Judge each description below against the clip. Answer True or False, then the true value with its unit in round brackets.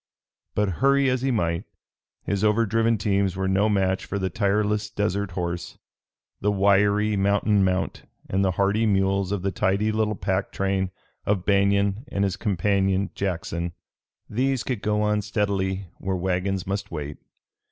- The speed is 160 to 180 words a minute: False (150 wpm)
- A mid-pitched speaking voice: False (100 Hz)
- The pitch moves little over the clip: True (1.7 semitones)